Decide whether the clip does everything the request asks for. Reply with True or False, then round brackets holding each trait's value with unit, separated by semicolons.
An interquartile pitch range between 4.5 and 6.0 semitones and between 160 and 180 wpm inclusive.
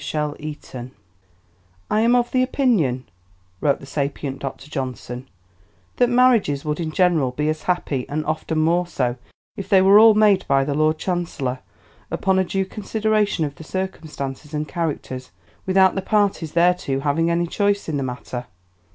True (5.6 semitones; 165 wpm)